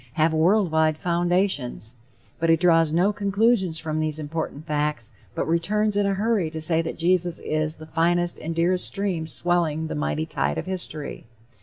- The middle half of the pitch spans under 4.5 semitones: Yes, narrow, 2.6 semitones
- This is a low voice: No, medium, 165 Hz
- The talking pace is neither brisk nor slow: Yes, average, 175 wpm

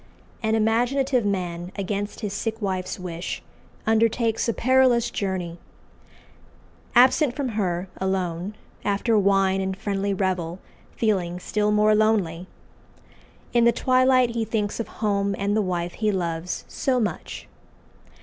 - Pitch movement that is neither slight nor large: Yes, average, 3.5 semitones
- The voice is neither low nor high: No, high, 205 Hz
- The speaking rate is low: Yes, slow, 130 wpm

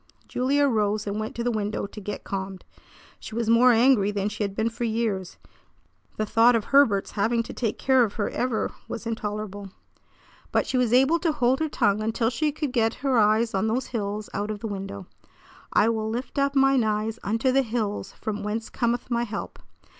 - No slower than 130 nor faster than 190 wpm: No, fast, 205 wpm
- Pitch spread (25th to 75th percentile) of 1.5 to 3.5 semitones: Yes, average, 2.9 semitones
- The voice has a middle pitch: No, high, 225 Hz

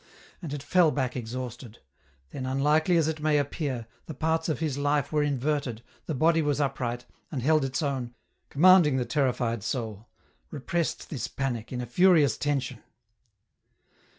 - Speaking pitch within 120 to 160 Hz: Yes, medium, 140 Hz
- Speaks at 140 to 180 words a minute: Yes, average, 155 wpm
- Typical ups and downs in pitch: Yes, average, 3.7 semitones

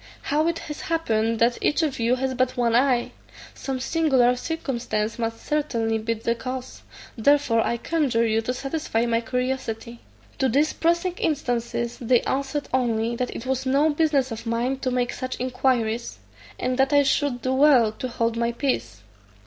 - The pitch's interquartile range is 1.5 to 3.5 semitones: Yes, average, 3.0 semitones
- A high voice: Yes, very high, 250 Hz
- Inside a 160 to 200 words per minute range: Yes, average, 175 wpm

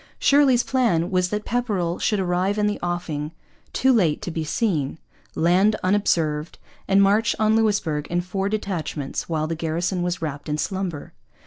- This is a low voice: No, medium, 180 Hz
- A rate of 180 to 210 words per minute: No, average, 160 wpm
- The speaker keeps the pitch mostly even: No, average, 4.3 semitones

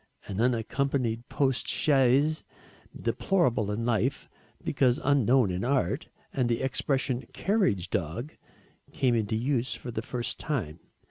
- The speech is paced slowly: Yes, slow, 125 wpm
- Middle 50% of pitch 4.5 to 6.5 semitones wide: No, average, 3.3 semitones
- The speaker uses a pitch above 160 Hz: No, low, 125 Hz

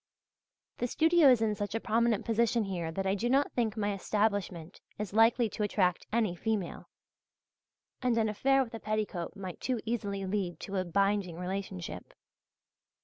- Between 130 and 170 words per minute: Yes, average, 165 wpm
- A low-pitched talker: No, high, 210 Hz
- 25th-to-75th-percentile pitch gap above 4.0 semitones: No, average, 3.0 semitones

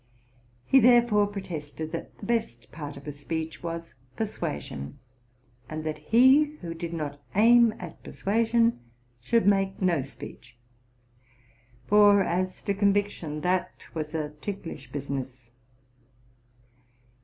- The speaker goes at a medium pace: No, slow, 120 wpm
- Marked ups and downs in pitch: Yes, wide, 5.7 semitones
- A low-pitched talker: No, medium, 175 Hz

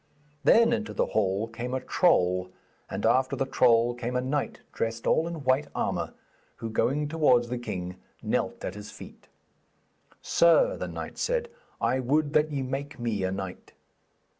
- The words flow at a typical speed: Yes, average, 165 wpm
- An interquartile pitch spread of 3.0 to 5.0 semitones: Yes, average, 4.7 semitones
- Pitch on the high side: No, low, 125 Hz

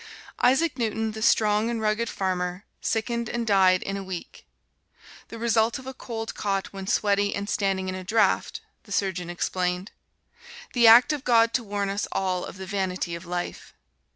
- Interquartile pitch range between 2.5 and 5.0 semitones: Yes, average, 3.3 semitones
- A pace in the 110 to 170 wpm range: No, average, 180 wpm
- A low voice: No, high, 205 Hz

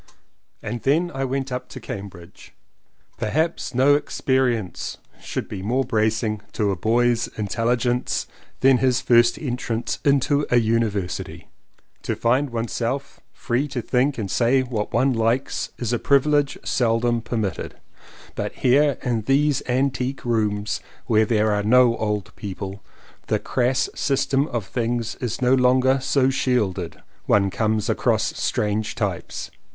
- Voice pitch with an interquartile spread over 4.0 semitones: No, average, 3.3 semitones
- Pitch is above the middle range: No, low, 120 Hz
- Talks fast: No, average, 145 wpm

